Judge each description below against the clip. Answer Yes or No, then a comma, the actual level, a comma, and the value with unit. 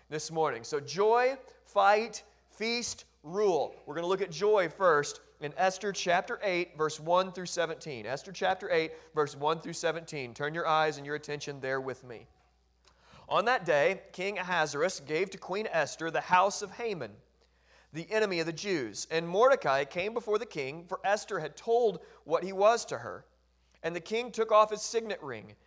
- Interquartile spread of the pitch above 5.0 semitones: Yes, wide, 5.4 semitones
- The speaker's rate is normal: Yes, average, 185 wpm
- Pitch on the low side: No, medium, 175 Hz